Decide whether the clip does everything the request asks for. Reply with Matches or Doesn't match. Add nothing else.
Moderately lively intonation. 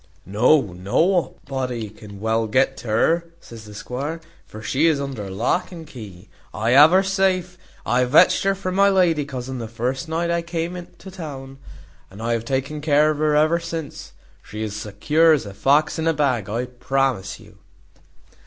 Doesn't match